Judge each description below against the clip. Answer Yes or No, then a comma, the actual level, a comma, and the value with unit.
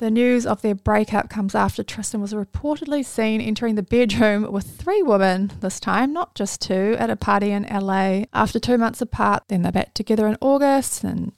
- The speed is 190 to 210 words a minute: Yes, average, 200 wpm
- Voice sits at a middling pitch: No, high, 215 Hz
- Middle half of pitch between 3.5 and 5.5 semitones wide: No, average, 3.1 semitones